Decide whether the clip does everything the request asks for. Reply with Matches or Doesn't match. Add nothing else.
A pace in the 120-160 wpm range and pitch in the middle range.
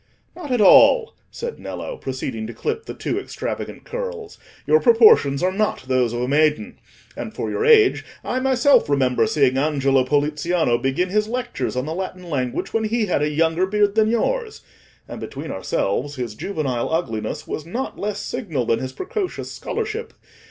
Doesn't match